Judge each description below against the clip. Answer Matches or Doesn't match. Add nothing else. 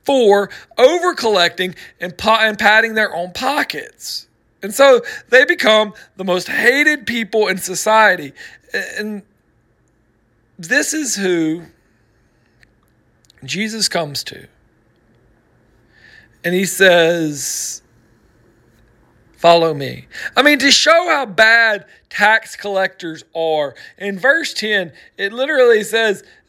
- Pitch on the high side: Matches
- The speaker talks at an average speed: Doesn't match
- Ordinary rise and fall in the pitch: Doesn't match